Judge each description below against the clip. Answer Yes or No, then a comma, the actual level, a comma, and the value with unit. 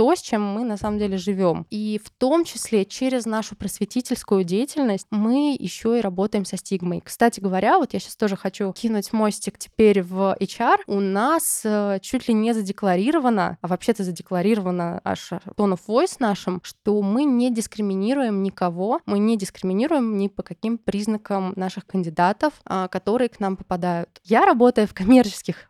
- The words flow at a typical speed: No, fast, 165 wpm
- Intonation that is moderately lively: Yes, average, 3.5 semitones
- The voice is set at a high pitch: Yes, high, 205 Hz